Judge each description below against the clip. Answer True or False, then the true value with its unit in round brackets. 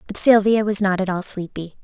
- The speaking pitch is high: True (195 Hz)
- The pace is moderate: False (230 wpm)